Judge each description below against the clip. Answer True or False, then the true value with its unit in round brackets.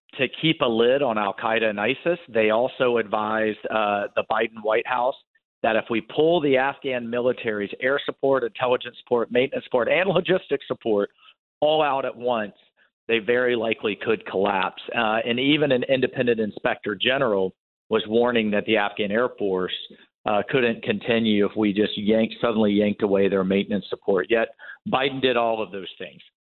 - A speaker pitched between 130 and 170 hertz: False (115 Hz)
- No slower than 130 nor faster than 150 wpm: False (175 wpm)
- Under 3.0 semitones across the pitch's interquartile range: False (3.4 semitones)